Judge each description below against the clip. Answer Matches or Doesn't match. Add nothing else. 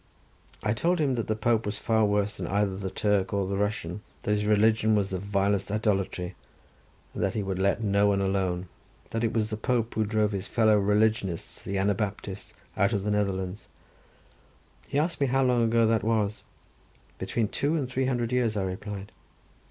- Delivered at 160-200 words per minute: Matches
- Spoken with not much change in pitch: Matches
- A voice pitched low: Matches